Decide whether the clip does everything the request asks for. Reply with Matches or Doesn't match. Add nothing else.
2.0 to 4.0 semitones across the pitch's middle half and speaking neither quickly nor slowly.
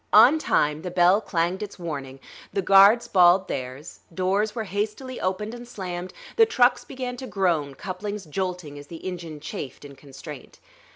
Doesn't match